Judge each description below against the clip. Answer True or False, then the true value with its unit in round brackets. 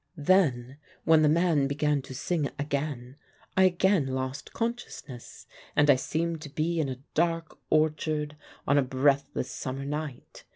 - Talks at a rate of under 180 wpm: True (150 wpm)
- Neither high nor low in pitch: True (150 Hz)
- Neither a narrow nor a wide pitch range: True (3.0 semitones)